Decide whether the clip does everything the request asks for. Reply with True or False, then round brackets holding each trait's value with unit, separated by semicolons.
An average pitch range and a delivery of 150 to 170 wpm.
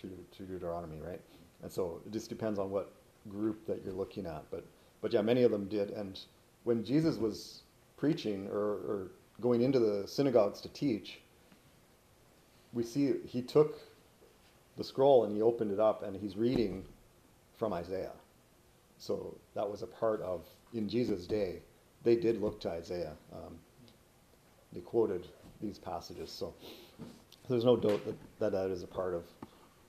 True (3.4 semitones; 165 wpm)